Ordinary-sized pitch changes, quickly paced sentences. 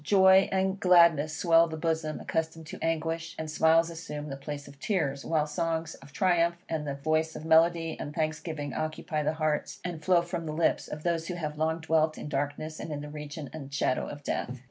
No: narrow, 1.8 semitones; fast, 210 wpm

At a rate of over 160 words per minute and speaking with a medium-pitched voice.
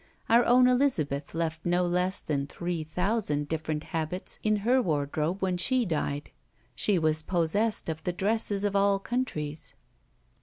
No: average, 150 wpm; medium, 175 Hz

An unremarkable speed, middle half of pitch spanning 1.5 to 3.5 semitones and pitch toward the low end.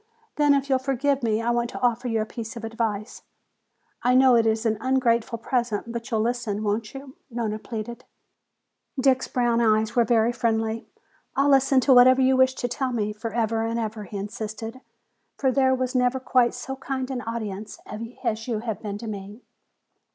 No: average, 190 wpm; average, 2.7 semitones; high, 235 Hz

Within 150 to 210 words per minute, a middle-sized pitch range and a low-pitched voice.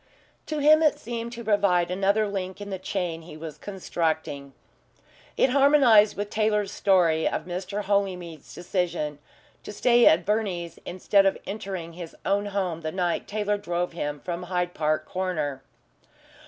No: average, 155 wpm; average, 3.3 semitones; medium, 185 Hz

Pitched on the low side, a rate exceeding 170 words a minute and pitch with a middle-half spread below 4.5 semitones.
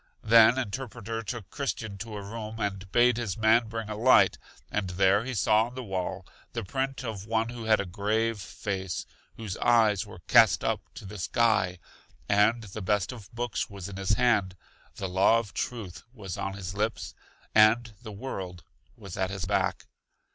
Yes: low, 110 Hz; average, 185 wpm; average, 2.9 semitones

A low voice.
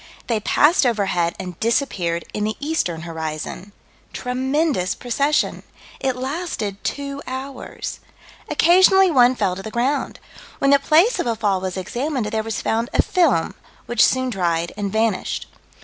No: high, 235 Hz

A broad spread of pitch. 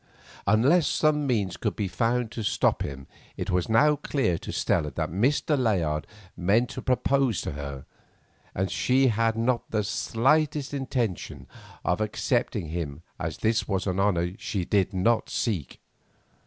Yes: wide, 6.0 semitones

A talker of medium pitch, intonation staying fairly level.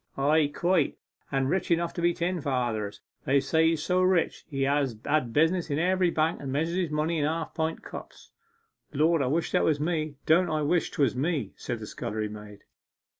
No: medium, 155 Hz; average, 3.6 semitones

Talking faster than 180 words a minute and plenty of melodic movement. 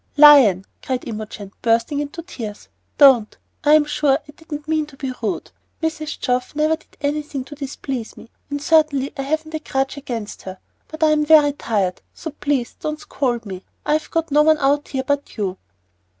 No: average, 190 wpm; average, 3.7 semitones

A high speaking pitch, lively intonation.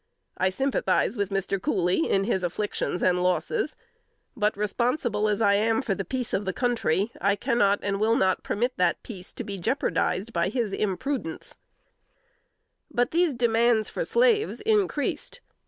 No: high, 210 Hz; average, 4.3 semitones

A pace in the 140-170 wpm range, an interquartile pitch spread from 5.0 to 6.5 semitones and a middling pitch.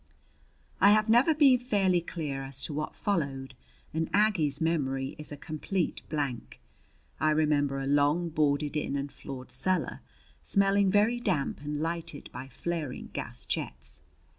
Yes: average, 145 wpm; average, 5.3 semitones; medium, 155 Hz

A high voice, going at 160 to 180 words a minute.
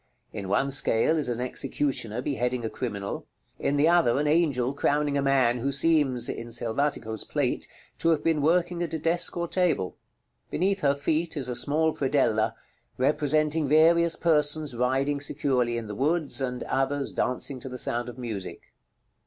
No: medium, 140 Hz; average, 170 wpm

